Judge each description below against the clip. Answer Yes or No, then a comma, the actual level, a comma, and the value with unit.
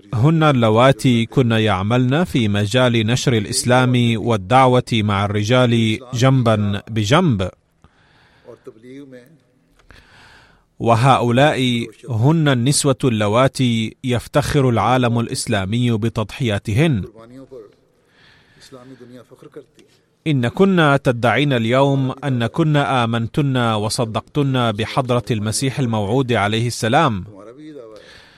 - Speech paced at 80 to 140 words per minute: No, average, 70 wpm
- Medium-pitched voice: No, low, 125 Hz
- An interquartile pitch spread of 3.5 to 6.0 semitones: No, average, 3.1 semitones